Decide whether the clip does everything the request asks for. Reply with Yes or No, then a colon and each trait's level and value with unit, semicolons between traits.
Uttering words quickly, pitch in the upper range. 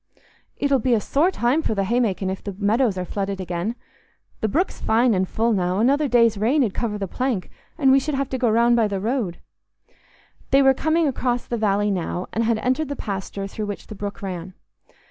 Yes: fast, 215 wpm; high, 225 Hz